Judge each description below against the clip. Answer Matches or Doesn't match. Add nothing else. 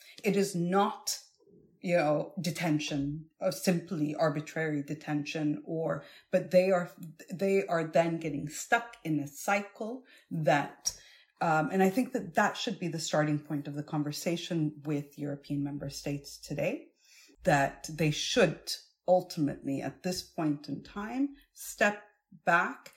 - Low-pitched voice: Doesn't match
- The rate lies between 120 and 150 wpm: Matches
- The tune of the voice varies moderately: Matches